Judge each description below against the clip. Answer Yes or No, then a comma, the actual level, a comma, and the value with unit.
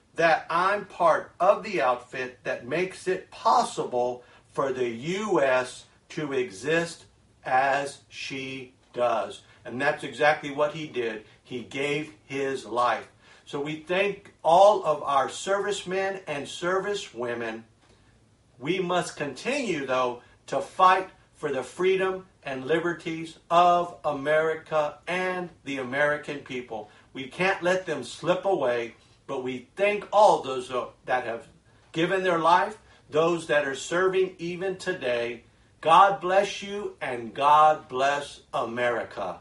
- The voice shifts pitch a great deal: Yes, wide, 6.2 semitones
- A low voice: No, medium, 145 Hz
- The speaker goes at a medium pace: No, slow, 125 wpm